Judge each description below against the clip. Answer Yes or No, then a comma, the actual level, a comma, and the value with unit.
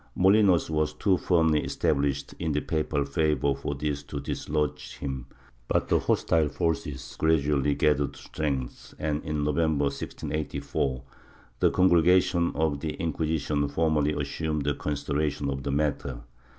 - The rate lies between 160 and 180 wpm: No, slow, 135 wpm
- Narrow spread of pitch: Yes, narrow, 2.0 semitones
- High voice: No, very low, 75 Hz